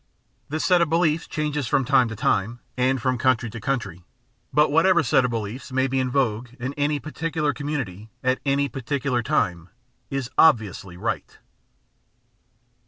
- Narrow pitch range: No, average, 4.1 semitones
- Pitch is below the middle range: Yes, low, 130 Hz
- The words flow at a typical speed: Yes, average, 165 wpm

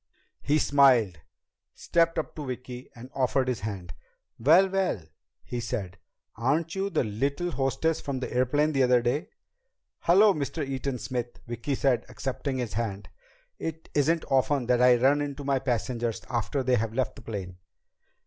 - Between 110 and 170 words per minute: Yes, average, 160 wpm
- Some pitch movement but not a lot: Yes, average, 3.5 semitones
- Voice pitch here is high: No, low, 130 Hz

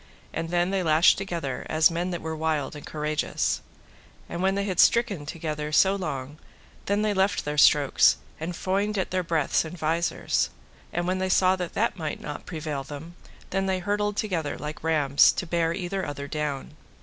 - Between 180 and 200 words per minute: Yes, average, 185 wpm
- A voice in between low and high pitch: Yes, medium, 165 Hz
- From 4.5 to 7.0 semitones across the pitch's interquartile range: No, average, 3.8 semitones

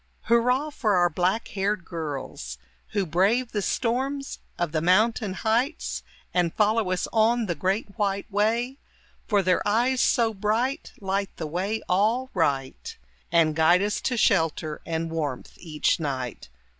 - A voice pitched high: Yes, high, 200 Hz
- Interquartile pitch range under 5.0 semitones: No, wide, 5.5 semitones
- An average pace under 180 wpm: Yes, average, 145 wpm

